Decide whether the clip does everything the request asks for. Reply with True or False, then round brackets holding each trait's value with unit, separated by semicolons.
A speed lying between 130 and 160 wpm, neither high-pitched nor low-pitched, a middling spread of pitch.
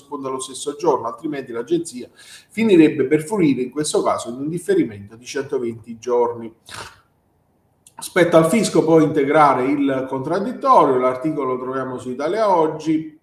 True (135 wpm; 145 Hz; 4.0 semitones)